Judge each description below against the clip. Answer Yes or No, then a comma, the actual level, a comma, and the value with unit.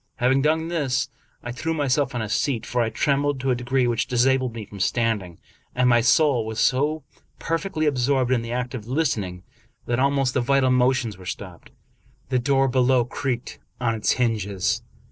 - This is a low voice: Yes, low, 125 Hz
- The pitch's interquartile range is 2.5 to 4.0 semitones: Yes, average, 2.8 semitones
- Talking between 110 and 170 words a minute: No, average, 185 wpm